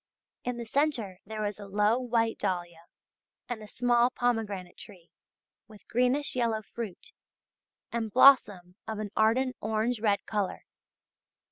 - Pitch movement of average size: Yes, average, 3.0 semitones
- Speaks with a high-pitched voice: Yes, high, 220 Hz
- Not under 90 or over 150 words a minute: Yes, slow, 135 wpm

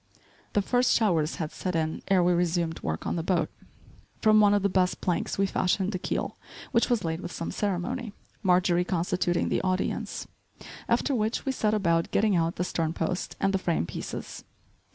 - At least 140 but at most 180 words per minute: No, average, 190 wpm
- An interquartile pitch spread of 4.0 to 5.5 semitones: No, average, 3.3 semitones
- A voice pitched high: No, medium, 180 Hz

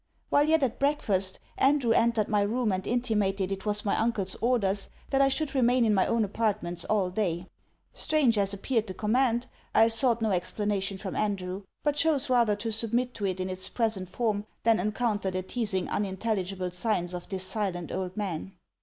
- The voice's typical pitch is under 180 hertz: No, high, 210 Hz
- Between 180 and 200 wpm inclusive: Yes, average, 185 wpm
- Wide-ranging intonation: No, average, 3.8 semitones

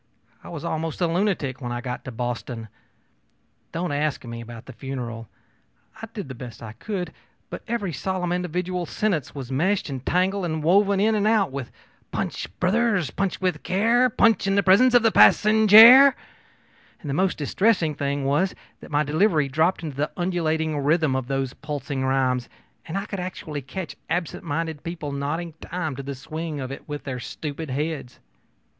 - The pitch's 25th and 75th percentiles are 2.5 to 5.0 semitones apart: No, wide, 5.6 semitones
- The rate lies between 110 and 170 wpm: No, average, 180 wpm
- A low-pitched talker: No, medium, 160 Hz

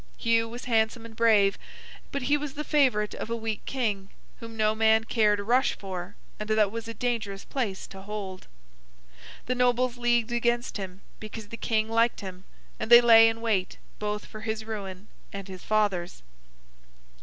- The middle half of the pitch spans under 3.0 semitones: Yes, narrow, 2.6 semitones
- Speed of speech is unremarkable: Yes, average, 180 wpm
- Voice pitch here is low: No, high, 220 Hz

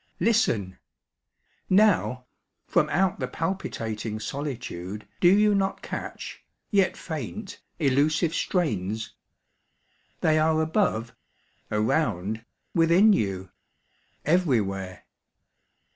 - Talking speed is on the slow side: Yes, slow, 85 wpm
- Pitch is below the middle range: No, medium, 155 Hz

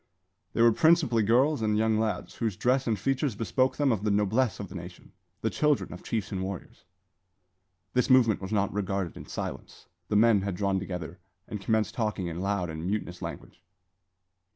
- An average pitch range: Yes, average, 3.4 semitones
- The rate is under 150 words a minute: No, average, 185 wpm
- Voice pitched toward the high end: No, low, 105 Hz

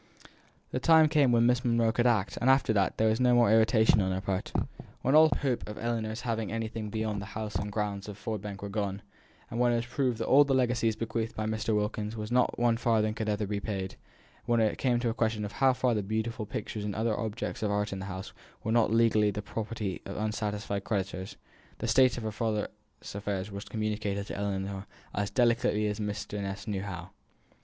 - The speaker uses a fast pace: Yes, fast, 215 wpm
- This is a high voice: No, low, 110 Hz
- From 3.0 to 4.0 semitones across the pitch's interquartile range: No, narrow, 2.4 semitones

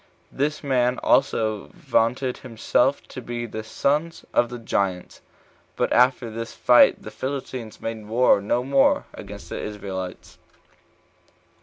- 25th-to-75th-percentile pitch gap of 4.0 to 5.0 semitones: No, average, 3.0 semitones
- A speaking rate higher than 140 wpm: No, slow, 135 wpm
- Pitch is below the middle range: Yes, low, 120 Hz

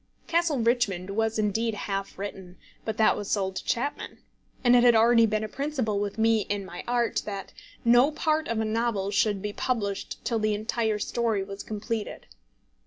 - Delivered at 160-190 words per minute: Yes, average, 180 wpm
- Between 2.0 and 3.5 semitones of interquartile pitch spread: Yes, average, 2.7 semitones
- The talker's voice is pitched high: Yes, high, 220 Hz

